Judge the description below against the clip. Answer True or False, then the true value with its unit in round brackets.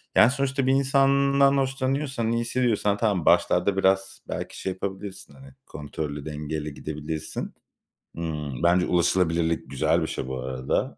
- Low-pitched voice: True (95 Hz)